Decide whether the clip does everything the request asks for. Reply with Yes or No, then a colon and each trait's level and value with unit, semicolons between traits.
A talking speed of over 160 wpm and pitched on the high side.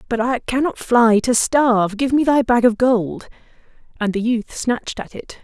Yes: average, 200 wpm; high, 240 Hz